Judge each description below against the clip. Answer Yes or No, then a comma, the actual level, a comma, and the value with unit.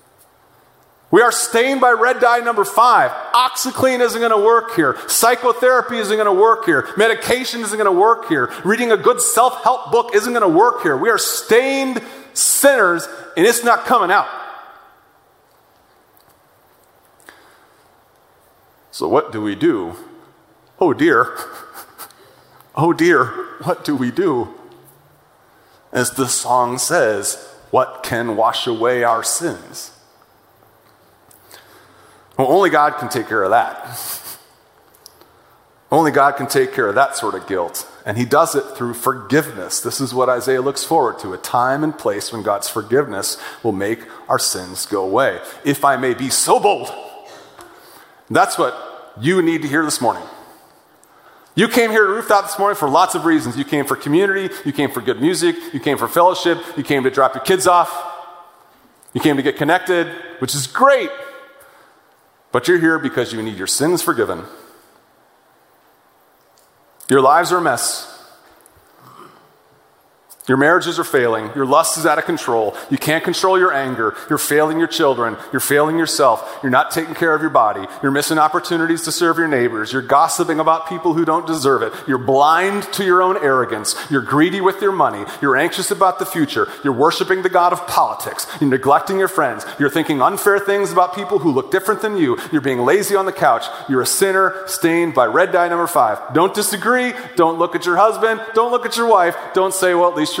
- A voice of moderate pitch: Yes, medium, 180 Hz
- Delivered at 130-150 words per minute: No, average, 175 wpm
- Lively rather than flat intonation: Yes, wide, 7.5 semitones